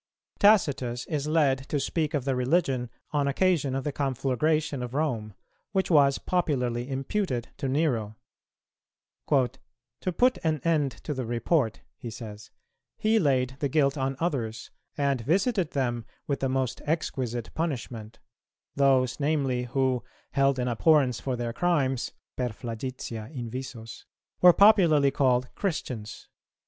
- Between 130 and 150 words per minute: Yes, slow, 135 wpm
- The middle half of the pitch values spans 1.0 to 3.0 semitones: No, average, 3.8 semitones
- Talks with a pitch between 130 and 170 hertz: Yes, low, 135 Hz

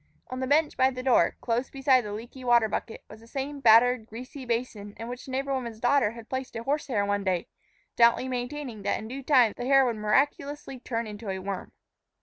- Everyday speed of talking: No, fast, 220 wpm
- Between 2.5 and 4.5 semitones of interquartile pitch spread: Yes, average, 3.2 semitones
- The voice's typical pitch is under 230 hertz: No, high, 245 Hz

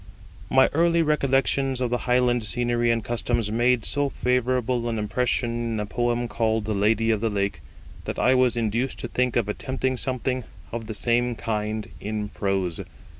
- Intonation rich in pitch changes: No, narrow, 2.4 semitones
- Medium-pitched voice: No, low, 120 Hz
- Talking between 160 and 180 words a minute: Yes, average, 175 wpm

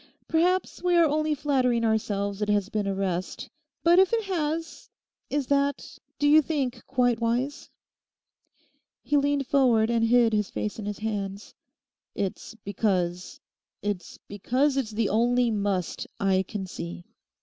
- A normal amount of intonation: No, wide, 5.9 semitones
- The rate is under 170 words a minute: Yes, average, 140 wpm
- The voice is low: No, high, 230 Hz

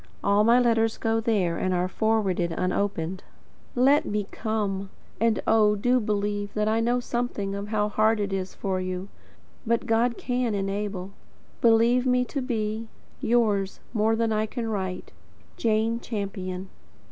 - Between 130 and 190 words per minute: Yes, average, 150 wpm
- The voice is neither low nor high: No, high, 215 Hz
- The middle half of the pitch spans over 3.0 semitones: No, average, 2.7 semitones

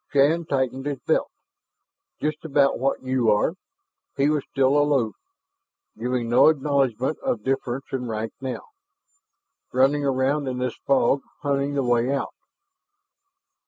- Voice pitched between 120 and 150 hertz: Yes, low, 135 Hz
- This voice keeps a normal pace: No, slow, 130 wpm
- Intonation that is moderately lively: No, narrow, 2.2 semitones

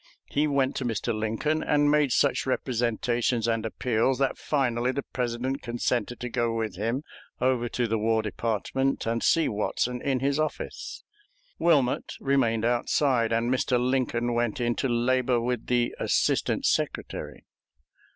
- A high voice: No, low, 120 Hz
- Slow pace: No, average, 150 wpm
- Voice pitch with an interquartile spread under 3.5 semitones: Yes, narrow, 2.4 semitones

